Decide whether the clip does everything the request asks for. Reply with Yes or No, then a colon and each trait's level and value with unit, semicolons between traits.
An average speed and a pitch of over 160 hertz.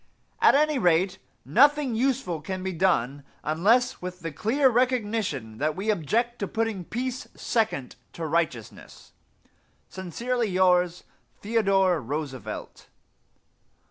No: slow, 110 wpm; high, 190 Hz